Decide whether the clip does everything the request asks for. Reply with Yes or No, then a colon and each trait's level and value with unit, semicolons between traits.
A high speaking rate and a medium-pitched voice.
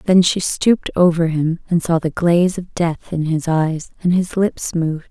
Yes: fast, 210 wpm; medium, 170 Hz